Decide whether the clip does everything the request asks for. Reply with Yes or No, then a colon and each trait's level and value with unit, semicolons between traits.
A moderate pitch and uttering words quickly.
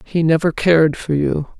No: medium, 160 Hz; average, 190 wpm